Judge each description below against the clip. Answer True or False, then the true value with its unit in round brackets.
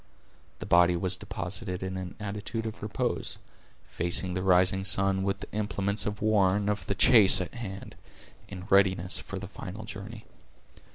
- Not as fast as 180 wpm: True (165 wpm)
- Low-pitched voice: True (95 Hz)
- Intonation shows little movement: True (1.9 semitones)